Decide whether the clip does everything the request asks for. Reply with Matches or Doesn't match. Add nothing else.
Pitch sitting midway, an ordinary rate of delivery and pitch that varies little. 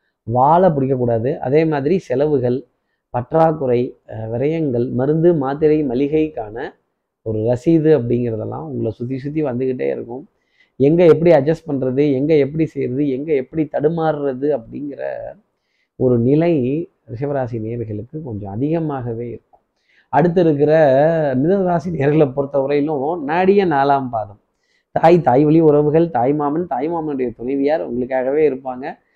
Doesn't match